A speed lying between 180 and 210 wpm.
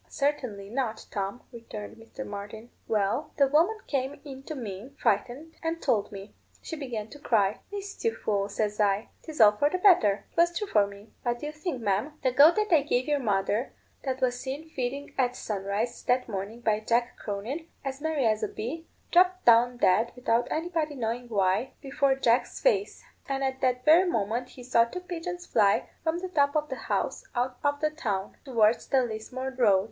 Yes: average, 195 wpm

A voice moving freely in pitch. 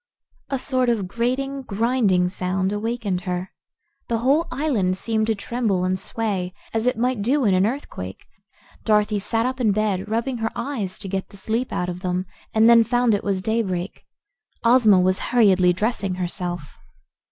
No: average, 4.2 semitones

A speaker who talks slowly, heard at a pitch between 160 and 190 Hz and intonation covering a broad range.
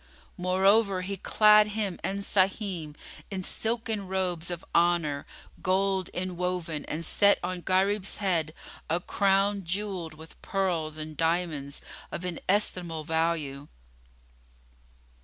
No: slow, 110 wpm; medium, 185 Hz; average, 3.2 semitones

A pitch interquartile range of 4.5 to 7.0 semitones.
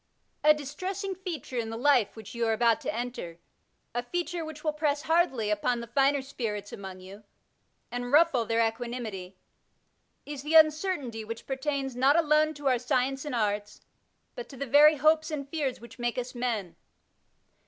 Yes: average, 4.8 semitones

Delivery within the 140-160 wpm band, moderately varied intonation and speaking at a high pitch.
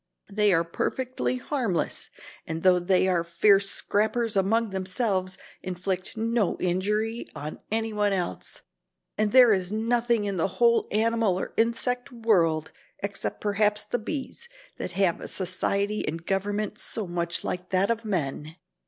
Yes: average, 145 wpm; average, 3.6 semitones; high, 200 Hz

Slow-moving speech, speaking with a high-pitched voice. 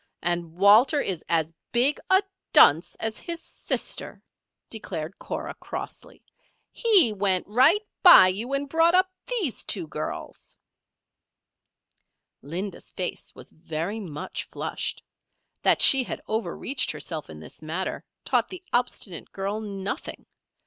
Yes: slow, 125 wpm; high, 205 Hz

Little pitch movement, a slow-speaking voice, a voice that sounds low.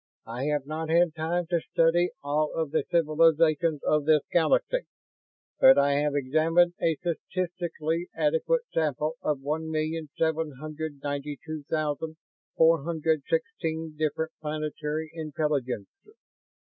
No: narrow, 1.6 semitones; slow, 130 wpm; medium, 155 Hz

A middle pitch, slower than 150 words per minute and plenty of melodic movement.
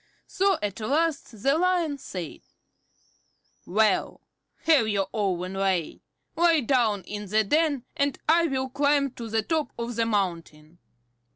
No: high, 235 Hz; slow, 135 wpm; wide, 6.8 semitones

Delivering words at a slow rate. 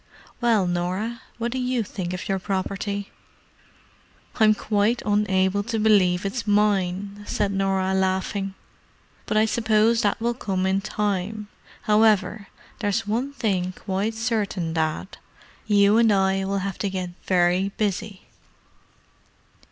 Yes: slow, 130 wpm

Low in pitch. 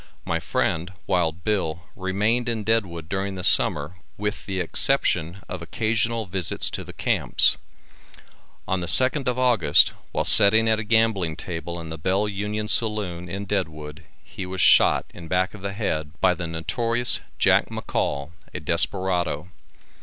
Yes: very low, 95 Hz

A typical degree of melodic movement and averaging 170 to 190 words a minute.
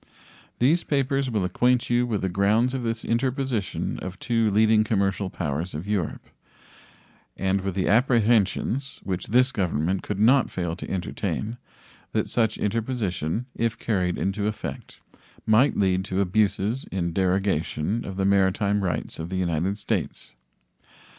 No: average, 3.8 semitones; average, 145 wpm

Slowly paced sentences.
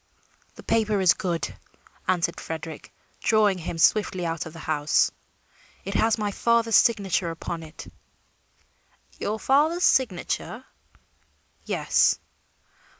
Yes: slow, 110 wpm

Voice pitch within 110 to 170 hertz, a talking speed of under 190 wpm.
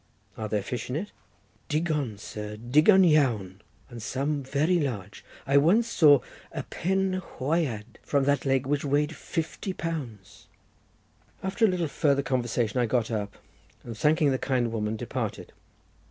Yes: medium, 140 Hz; average, 150 wpm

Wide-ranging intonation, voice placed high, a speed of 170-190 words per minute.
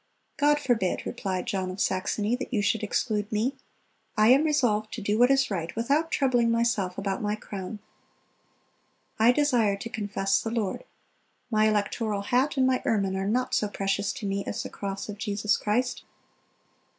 No: average, 3.5 semitones; high, 215 Hz; average, 175 wpm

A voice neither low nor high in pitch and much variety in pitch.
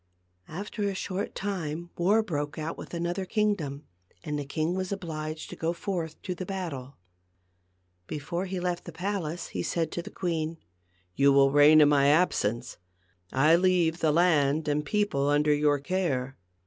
No: medium, 165 Hz; average, 3.7 semitones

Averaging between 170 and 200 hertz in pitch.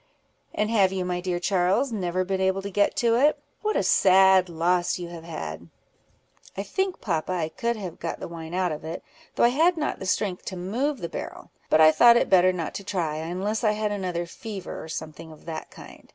Yes: medium, 185 Hz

